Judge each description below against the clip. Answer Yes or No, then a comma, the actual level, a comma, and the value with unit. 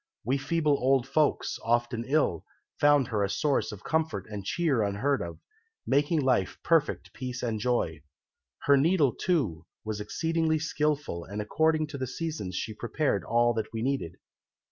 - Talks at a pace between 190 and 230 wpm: No, average, 160 wpm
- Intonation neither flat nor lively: No, wide, 5.8 semitones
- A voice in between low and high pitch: No, low, 130 Hz